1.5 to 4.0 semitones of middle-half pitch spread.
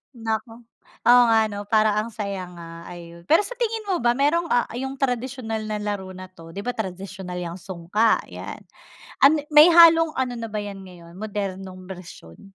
No: average, 5.0 semitones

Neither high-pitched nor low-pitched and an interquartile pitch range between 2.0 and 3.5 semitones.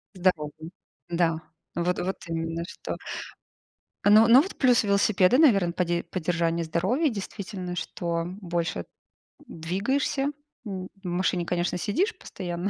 Yes: medium, 180 Hz; average, 3.2 semitones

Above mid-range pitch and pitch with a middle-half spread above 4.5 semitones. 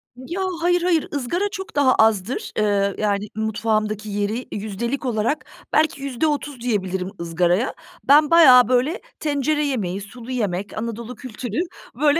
Yes: high, 240 Hz; wide, 5.6 semitones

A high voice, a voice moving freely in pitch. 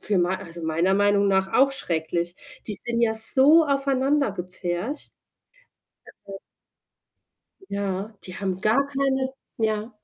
Yes: high, 205 Hz; wide, 6.2 semitones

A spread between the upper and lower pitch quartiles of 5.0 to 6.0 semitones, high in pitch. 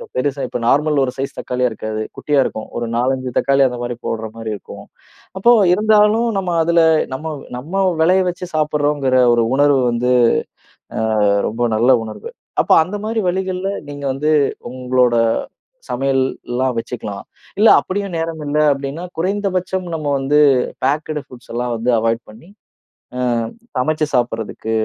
No: wide, 5.5 semitones; medium, 140 Hz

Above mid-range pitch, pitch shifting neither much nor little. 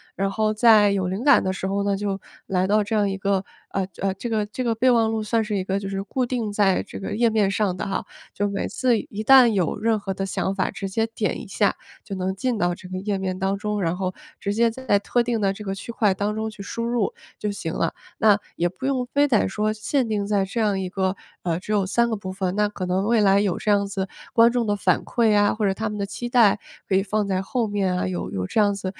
No: high, 205 Hz; narrow, 2.3 semitones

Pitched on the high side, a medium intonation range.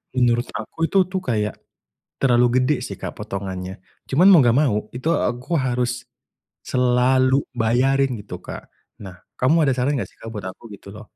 No: low, 125 Hz; average, 3.3 semitones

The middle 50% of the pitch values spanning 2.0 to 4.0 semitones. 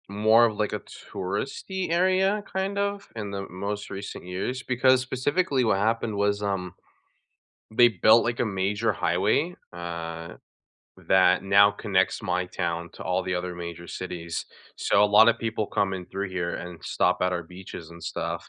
No: average, 4.4 semitones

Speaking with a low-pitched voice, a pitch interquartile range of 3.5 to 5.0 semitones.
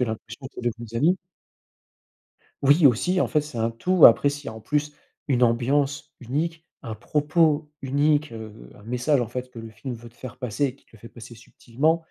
Yes: low, 130 Hz; average, 4.2 semitones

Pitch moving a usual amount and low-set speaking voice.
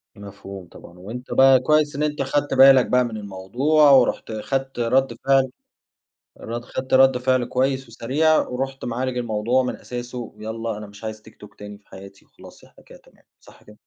Yes: average, 3.7 semitones; low, 125 Hz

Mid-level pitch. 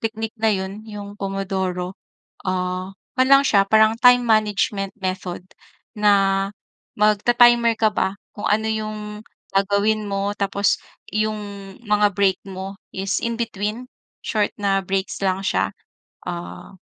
No: high, 205 Hz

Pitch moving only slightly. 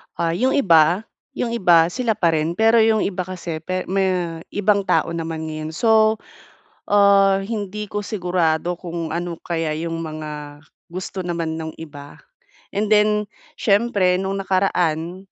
No: average, 3.7 semitones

